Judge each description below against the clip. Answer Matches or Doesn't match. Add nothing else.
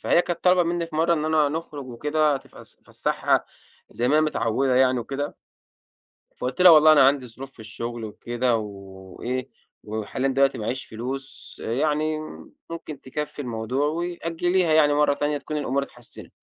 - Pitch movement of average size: Matches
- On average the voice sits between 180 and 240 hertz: Doesn't match